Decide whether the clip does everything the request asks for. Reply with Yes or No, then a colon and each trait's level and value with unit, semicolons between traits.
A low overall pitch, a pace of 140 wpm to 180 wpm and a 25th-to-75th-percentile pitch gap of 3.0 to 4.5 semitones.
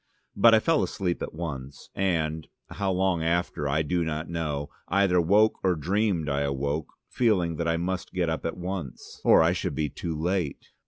No: very low, 85 Hz; average, 190 wpm; average, 3.3 semitones